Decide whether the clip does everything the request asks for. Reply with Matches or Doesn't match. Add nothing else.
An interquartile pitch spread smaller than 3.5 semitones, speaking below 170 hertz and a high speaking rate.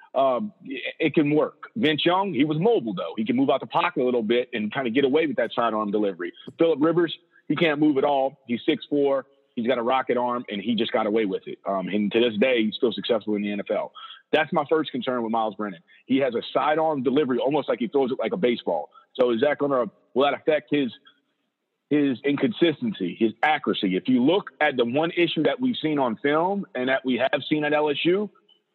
Doesn't match